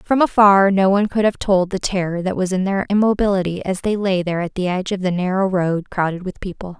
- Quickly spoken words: Yes, fast, 245 wpm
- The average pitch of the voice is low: No, high, 190 Hz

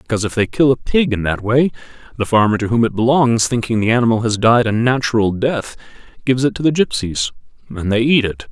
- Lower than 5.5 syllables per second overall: No, 6.0 syllables/s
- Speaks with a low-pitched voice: Yes, low, 115 Hz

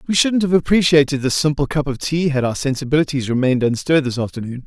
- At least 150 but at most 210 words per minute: Yes, fast, 205 wpm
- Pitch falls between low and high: Yes, medium, 145 Hz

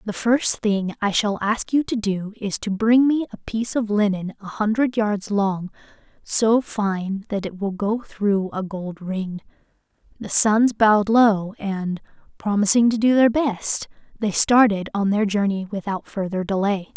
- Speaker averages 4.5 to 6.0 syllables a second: No, 4.2 syllables/s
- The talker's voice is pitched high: Yes, high, 210 Hz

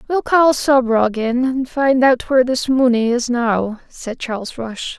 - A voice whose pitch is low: No, very high, 250 Hz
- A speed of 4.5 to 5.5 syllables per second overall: No, 4.0 syllables/s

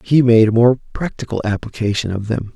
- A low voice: Yes, low, 115 Hz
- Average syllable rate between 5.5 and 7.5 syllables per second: Yes, 5.6 syllables/s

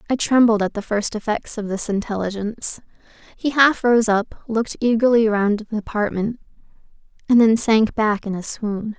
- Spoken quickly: No, average, 165 wpm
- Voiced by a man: No, female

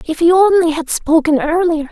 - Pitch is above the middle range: Yes, very high, 325 Hz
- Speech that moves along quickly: No, average, 190 wpm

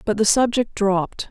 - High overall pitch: Yes, high, 210 Hz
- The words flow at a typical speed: Yes, average, 185 wpm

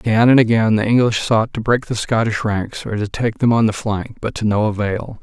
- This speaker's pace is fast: Yes, fast, 250 wpm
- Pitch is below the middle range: Yes, low, 110 Hz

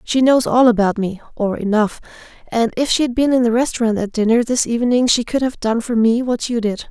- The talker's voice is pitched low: No, high, 235 Hz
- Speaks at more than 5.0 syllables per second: Yes, 5.5 syllables/s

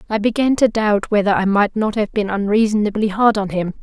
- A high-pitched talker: Yes, high, 210 Hz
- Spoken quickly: Yes, fast, 220 wpm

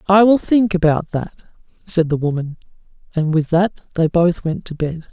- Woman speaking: No, male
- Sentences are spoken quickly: No, average, 190 wpm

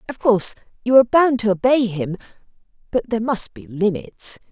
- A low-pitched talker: No, high, 220 Hz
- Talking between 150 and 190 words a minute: Yes, average, 160 wpm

